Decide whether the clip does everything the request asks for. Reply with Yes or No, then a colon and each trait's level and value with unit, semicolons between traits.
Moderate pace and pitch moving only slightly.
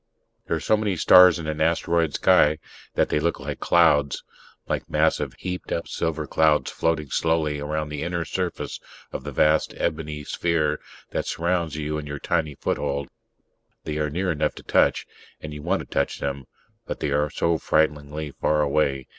Yes: average, 180 wpm; narrow, 2.1 semitones